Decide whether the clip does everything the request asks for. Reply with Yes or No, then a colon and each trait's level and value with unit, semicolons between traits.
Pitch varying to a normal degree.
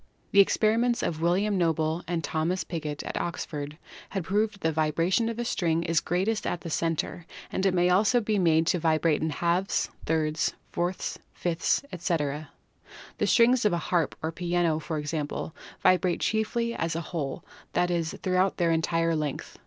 Yes: average, 3.0 semitones